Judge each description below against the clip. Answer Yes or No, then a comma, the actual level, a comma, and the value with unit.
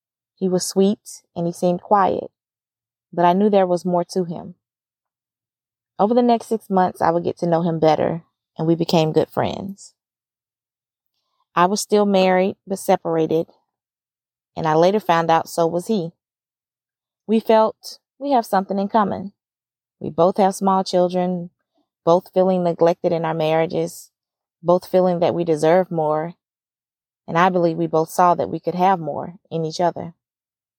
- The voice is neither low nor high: Yes, medium, 170 Hz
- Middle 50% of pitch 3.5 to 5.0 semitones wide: No, average, 3.1 semitones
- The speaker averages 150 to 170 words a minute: Yes, average, 165 wpm